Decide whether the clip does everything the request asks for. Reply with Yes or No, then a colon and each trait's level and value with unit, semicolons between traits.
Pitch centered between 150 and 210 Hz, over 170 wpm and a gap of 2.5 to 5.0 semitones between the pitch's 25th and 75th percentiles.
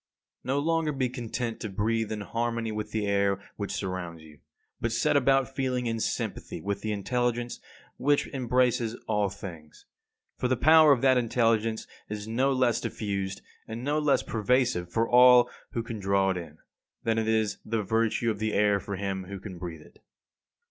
No: low, 110 Hz; average, 180 wpm; average, 3.8 semitones